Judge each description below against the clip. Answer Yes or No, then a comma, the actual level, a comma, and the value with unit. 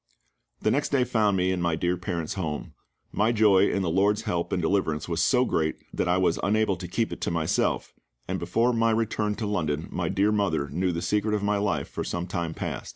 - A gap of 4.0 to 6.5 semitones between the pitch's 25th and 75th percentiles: No, average, 3.6 semitones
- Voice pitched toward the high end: No, very low, 95 Hz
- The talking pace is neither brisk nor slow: No, fast, 225 wpm